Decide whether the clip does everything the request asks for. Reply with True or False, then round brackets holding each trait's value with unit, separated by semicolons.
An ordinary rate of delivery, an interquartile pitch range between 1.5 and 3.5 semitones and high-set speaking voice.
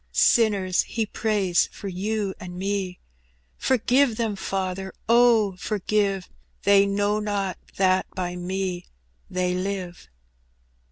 False (115 wpm; 2.4 semitones; 195 Hz)